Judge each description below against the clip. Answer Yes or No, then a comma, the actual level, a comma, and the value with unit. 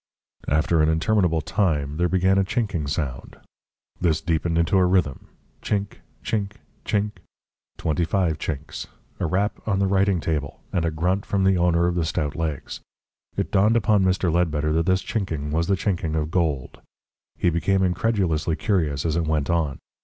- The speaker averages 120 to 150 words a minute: No, average, 170 wpm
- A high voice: No, very low, 85 Hz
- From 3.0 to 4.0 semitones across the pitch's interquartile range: Yes, average, 3.6 semitones